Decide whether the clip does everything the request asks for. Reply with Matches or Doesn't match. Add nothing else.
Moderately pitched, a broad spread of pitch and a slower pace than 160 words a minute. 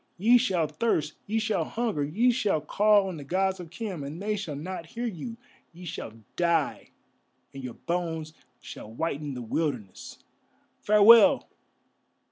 Matches